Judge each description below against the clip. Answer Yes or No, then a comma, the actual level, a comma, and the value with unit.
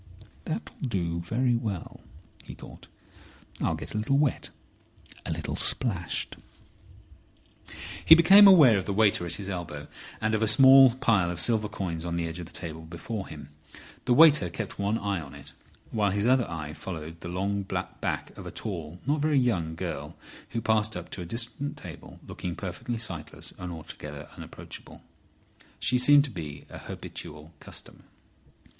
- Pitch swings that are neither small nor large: No, wide, 6.0 semitones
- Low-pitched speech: Yes, low, 100 Hz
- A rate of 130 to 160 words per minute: No, average, 170 wpm